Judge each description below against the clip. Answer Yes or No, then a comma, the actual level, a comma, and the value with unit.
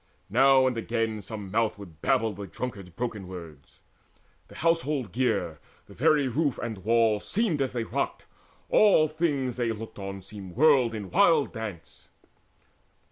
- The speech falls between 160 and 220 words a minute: No, average, 150 wpm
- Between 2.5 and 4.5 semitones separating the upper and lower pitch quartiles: No, average, 5.1 semitones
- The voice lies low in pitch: Yes, low, 115 Hz